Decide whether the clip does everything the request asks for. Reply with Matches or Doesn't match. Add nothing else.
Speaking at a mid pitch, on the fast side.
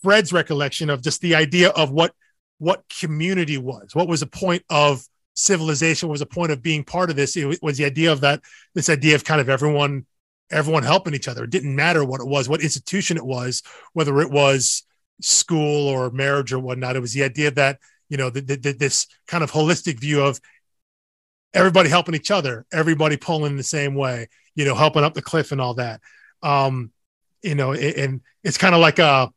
Matches